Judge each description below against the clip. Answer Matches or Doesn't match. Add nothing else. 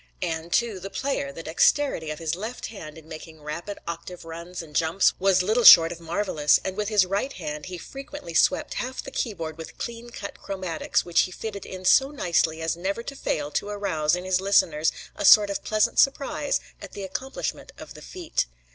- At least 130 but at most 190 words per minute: Doesn't match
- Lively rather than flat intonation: Doesn't match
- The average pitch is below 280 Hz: Matches